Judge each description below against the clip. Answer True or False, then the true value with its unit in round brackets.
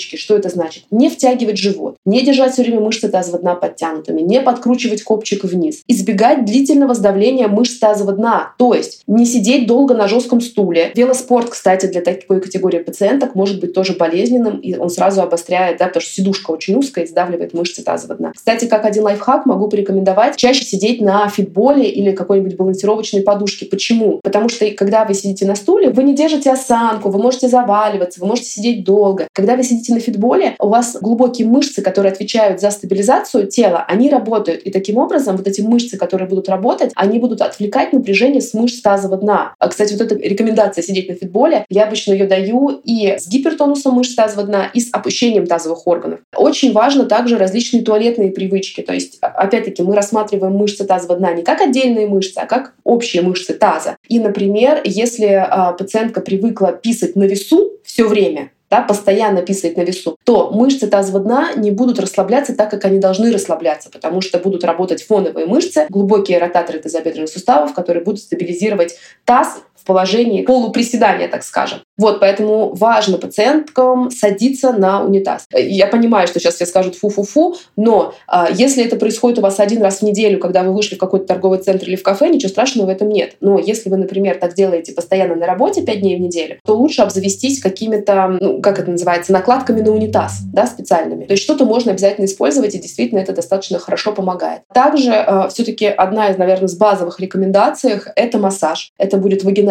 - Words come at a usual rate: False (185 wpm)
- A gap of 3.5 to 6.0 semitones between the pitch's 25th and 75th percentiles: True (3.8 semitones)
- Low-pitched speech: False (205 Hz)